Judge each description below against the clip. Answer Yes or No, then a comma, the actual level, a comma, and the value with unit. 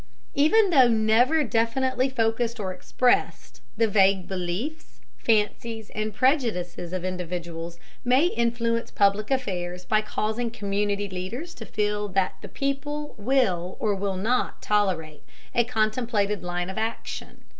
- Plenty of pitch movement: No, average, 4.4 semitones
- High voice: Yes, high, 215 Hz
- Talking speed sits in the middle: No, slow, 130 wpm